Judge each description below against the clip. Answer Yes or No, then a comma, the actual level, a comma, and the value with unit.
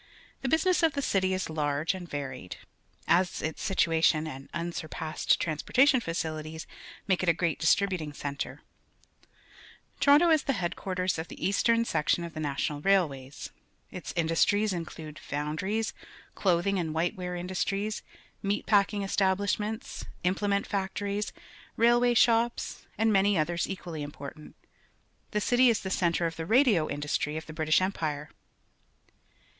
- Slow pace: No, average, 150 wpm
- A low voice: No, medium, 180 Hz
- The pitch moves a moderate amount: Yes, average, 4.5 semitones